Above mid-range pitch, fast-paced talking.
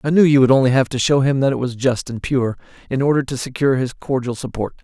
No: low, 130 Hz; fast, 275 wpm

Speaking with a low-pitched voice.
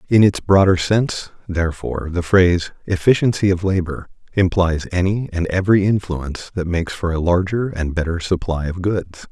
Yes: very low, 90 Hz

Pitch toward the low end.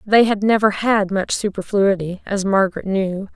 No: high, 200 Hz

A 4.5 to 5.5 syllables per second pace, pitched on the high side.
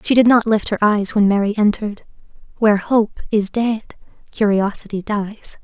Yes: 5.0 syllables/s; high, 210 Hz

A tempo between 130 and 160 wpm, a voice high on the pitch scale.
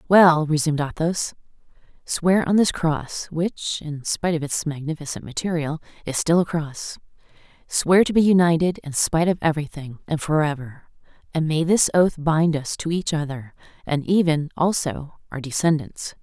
No: average, 155 wpm; medium, 160 Hz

